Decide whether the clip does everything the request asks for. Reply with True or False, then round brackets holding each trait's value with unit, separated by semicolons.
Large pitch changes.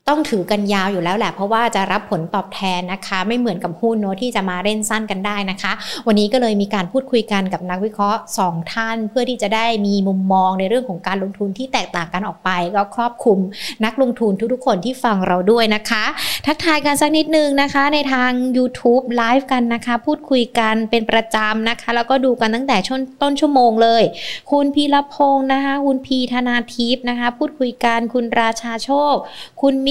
False (4.3 semitones)